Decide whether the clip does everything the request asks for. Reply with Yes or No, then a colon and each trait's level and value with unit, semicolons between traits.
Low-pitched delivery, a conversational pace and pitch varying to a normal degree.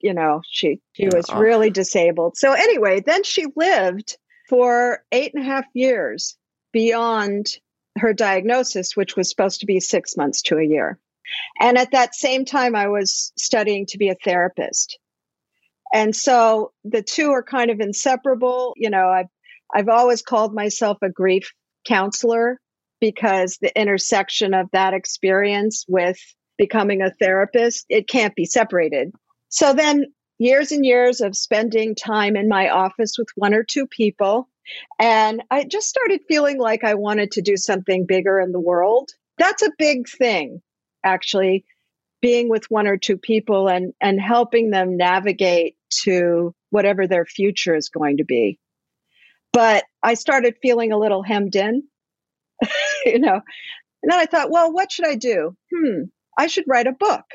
No: high, 220 Hz; average, 160 wpm; average, 4.7 semitones